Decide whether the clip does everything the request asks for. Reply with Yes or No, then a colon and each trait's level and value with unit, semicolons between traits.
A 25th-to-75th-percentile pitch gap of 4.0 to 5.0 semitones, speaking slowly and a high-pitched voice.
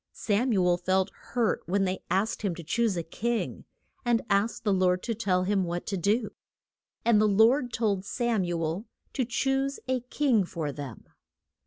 No: average, 4.4 semitones; average, 185 wpm; high, 205 Hz